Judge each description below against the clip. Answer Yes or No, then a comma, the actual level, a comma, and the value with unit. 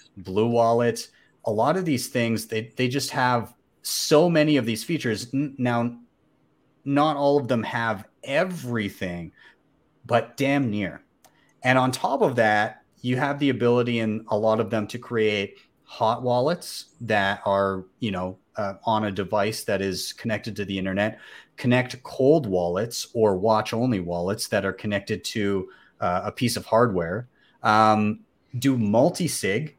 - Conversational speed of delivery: Yes, average, 155 wpm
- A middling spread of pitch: Yes, average, 3.4 semitones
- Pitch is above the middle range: No, low, 115 Hz